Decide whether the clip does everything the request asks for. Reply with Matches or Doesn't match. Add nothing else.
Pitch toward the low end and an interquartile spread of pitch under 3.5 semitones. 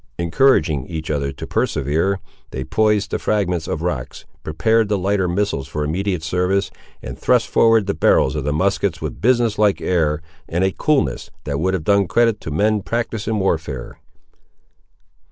Doesn't match